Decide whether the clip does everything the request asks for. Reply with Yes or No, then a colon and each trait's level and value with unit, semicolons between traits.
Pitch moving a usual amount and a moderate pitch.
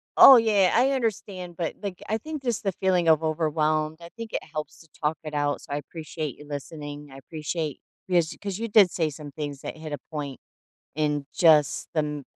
Yes: average, 4.0 semitones; medium, 160 Hz